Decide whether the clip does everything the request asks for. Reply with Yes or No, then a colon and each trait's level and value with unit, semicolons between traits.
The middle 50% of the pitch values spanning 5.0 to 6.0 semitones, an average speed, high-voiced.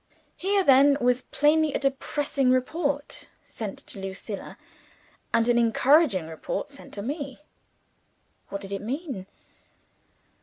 No: wide, 5.4 semitones; slow, 120 wpm; very high, 265 Hz